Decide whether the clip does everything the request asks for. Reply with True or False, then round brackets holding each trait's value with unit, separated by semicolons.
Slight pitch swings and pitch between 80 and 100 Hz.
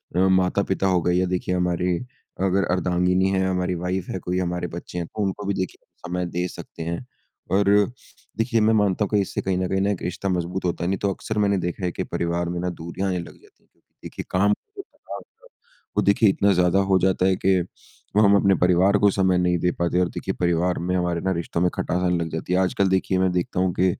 True (1.5 semitones; 90 Hz)